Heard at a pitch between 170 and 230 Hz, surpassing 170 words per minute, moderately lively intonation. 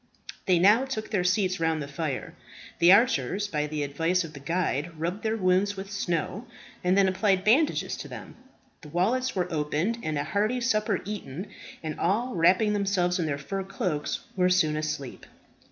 Yes: medium, 185 Hz; average, 180 wpm; average, 4.7 semitones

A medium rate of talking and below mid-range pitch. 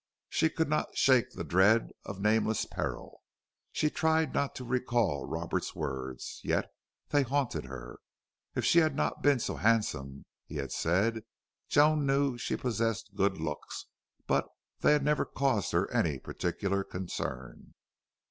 Yes: average, 150 wpm; low, 115 Hz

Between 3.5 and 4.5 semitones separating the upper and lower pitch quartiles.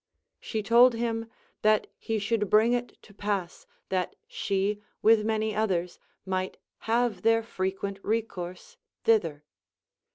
No: average, 3.0 semitones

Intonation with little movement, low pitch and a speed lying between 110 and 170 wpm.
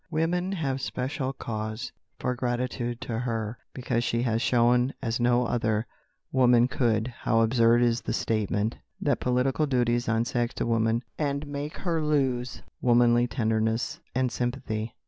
Yes: narrow, 2.2 semitones; low, 120 Hz; average, 145 wpm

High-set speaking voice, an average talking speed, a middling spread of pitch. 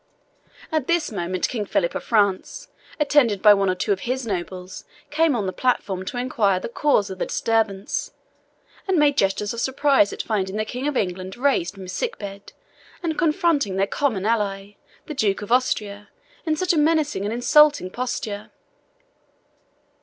No: high, 215 Hz; average, 175 wpm; wide, 6.6 semitones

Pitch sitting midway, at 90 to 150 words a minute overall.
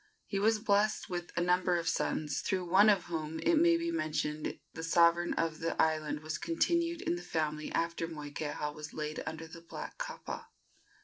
No: medium, 170 Hz; average, 185 wpm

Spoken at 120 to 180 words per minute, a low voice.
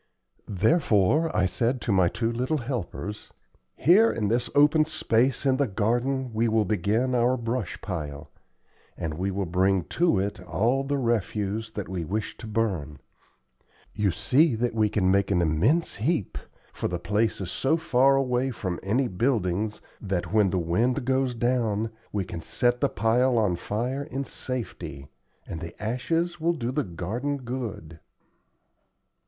Yes: average, 160 wpm; low, 115 Hz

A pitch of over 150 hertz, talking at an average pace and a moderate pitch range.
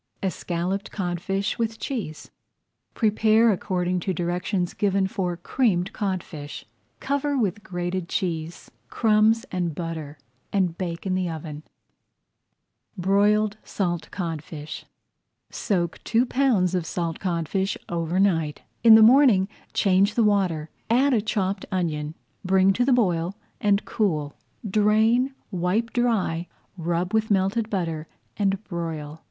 No: high, 190 Hz; slow, 125 wpm; average, 3.8 semitones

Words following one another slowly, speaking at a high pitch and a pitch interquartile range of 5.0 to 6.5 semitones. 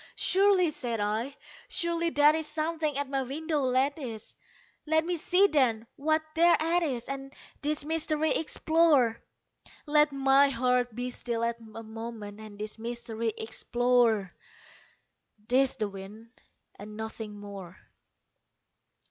Yes: slow, 120 wpm; very high, 260 Hz; wide, 5.5 semitones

